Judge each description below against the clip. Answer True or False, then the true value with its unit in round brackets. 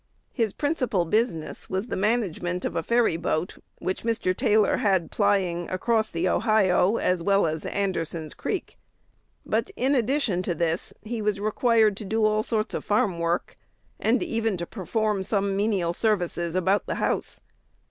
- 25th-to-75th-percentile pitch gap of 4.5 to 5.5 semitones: False (3.8 semitones)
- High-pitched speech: True (200 Hz)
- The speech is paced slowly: False (160 wpm)